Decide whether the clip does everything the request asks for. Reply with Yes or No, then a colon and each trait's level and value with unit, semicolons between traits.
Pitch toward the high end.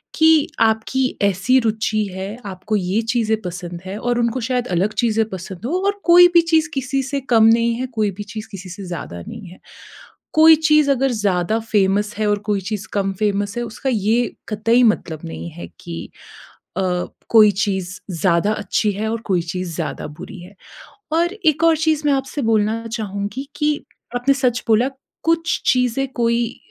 Yes: high, 220 Hz